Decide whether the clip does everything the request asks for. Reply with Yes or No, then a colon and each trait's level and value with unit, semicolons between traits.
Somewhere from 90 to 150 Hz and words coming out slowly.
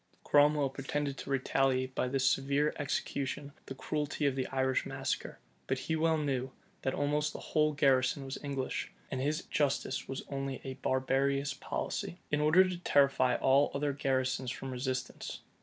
No: low, 135 Hz; average, 160 wpm